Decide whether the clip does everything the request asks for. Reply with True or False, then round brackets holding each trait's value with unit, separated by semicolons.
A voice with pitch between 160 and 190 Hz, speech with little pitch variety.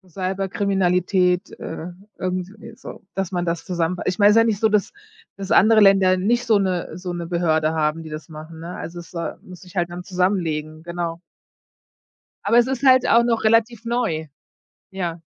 False (185 Hz; 3.4 semitones)